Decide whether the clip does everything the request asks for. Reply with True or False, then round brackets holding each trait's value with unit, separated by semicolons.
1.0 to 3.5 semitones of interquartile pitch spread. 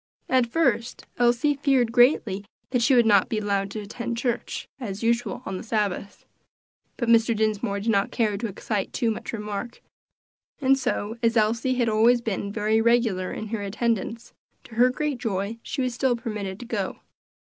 True (2.7 semitones)